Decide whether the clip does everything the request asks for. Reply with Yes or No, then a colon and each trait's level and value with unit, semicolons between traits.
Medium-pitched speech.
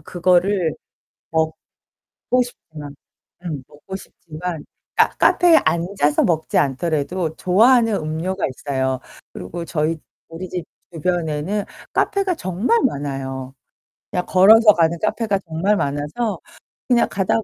Yes: medium, 175 Hz